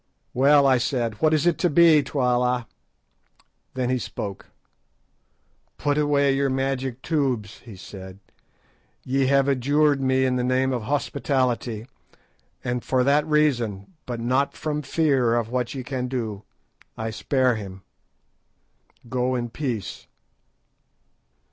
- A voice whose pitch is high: No, low, 130 Hz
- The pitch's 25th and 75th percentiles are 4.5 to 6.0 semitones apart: No, average, 2.8 semitones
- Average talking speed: No, slow, 130 wpm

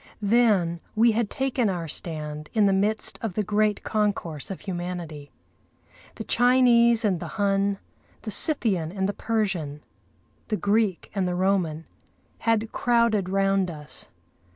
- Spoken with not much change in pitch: No, average, 4.0 semitones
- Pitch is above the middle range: Yes, high, 200 Hz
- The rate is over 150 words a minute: No, average, 140 wpm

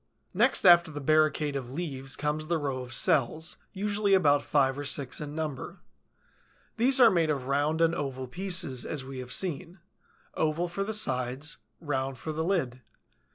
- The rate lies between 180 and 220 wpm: No, average, 170 wpm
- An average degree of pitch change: Yes, average, 4.3 semitones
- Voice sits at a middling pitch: Yes, medium, 150 Hz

